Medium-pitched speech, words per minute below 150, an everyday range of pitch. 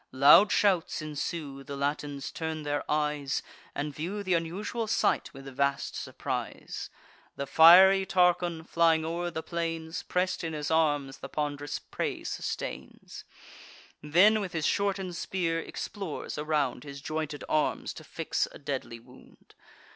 Yes: medium, 160 Hz; average, 140 wpm; average, 3.3 semitones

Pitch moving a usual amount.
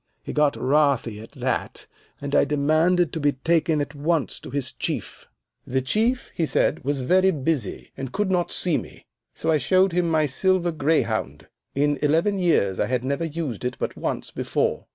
Yes: average, 4.2 semitones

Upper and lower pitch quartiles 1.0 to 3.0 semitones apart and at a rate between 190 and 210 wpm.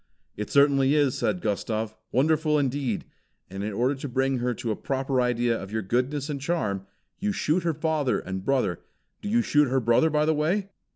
No: average, 4.5 semitones; average, 195 wpm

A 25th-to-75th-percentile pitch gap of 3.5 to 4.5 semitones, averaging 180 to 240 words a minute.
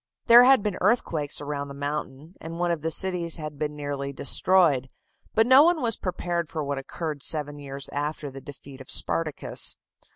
Yes: average, 4.0 semitones; average, 185 wpm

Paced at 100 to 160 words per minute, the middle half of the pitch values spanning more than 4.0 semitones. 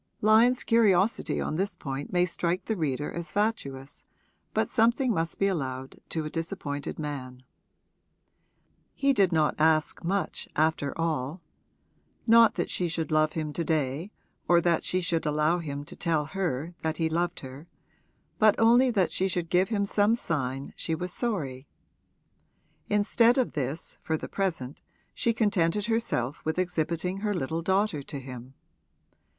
Yes: average, 155 wpm; average, 5.0 semitones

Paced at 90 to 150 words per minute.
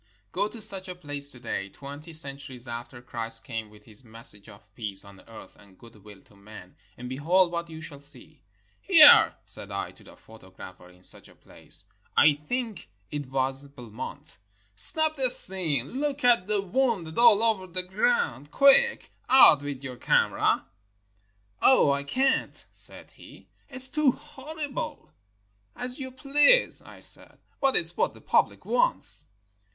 No: average, 165 wpm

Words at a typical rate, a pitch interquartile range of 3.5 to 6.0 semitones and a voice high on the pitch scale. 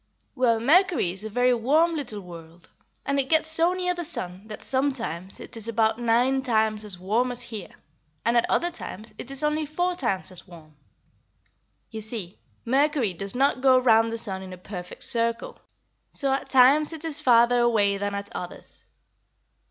Yes: average, 185 wpm; wide, 5.5 semitones; high, 235 Hz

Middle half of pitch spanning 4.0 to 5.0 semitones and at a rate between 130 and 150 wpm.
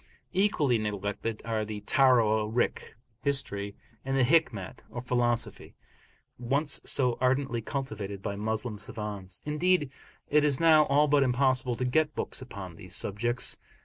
Yes: average, 4.7 semitones; slow, 135 wpm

